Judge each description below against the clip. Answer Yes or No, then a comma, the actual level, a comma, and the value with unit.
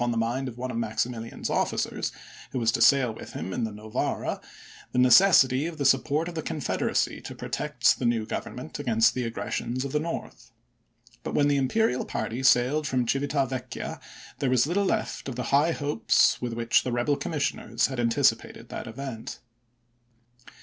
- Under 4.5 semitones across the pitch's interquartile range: Yes, average, 3.4 semitones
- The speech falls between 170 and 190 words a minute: Yes, average, 175 wpm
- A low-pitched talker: Yes, low, 130 Hz